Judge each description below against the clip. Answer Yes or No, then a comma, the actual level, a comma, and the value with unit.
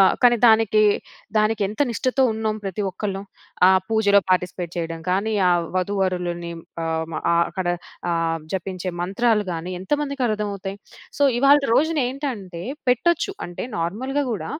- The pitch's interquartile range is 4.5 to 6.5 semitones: Yes, average, 4.8 semitones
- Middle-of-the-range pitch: No, high, 200 Hz